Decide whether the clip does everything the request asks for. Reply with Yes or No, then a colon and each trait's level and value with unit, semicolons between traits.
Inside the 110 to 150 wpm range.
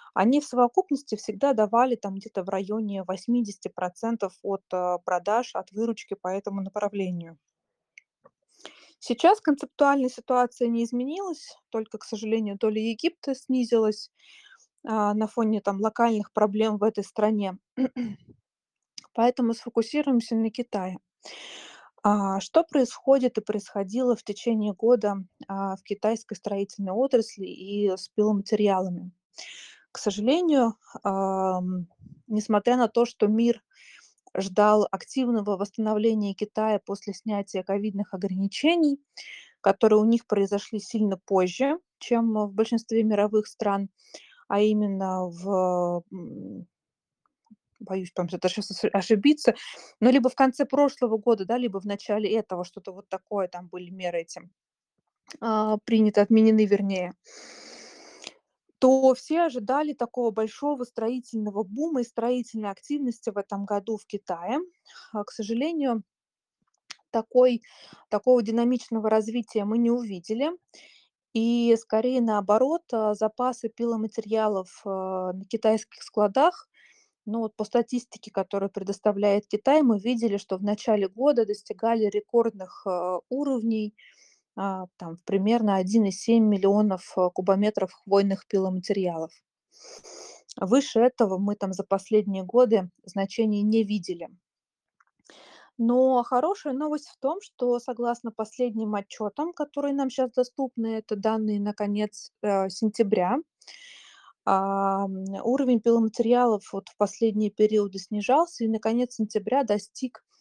Yes: average, 115 wpm